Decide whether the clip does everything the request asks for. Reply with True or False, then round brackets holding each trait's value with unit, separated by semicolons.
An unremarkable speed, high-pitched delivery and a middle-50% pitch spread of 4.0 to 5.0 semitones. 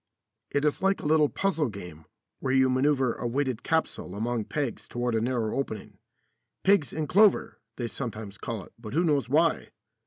False (180 wpm; 130 Hz; 4.7 semitones)